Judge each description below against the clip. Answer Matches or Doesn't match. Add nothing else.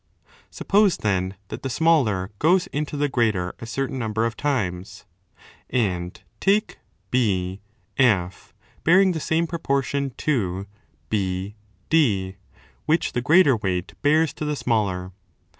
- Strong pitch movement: Matches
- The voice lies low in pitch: Matches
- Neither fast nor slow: Doesn't match